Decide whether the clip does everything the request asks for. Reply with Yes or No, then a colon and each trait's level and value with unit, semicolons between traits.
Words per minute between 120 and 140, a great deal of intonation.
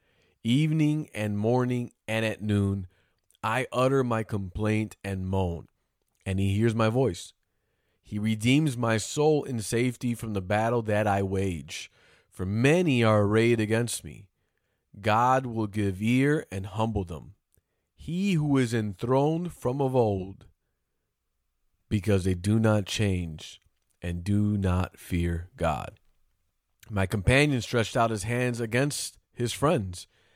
No: slow, 135 wpm; average, 4.1 semitones